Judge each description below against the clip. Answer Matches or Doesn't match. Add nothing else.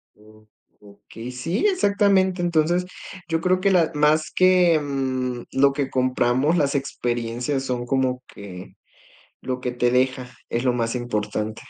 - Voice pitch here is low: Matches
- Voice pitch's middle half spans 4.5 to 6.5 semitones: Matches